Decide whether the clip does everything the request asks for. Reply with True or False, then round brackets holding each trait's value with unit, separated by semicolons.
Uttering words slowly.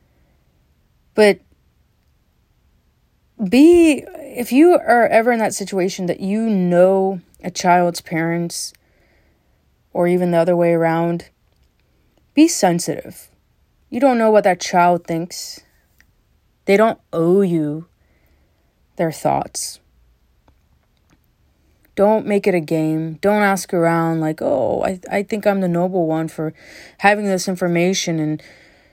True (120 wpm)